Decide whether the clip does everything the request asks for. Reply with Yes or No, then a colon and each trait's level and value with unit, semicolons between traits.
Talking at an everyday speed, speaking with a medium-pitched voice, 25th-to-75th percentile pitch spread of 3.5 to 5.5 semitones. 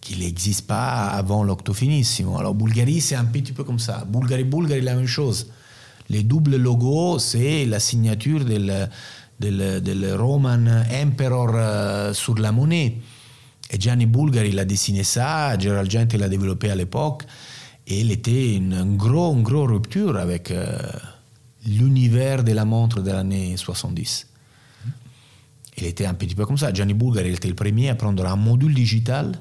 No: average, 165 wpm; low, 115 Hz; average, 4.1 semitones